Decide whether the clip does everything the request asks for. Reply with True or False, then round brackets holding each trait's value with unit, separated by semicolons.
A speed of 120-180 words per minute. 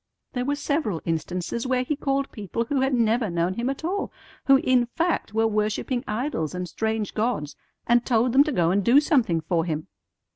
False (195 wpm)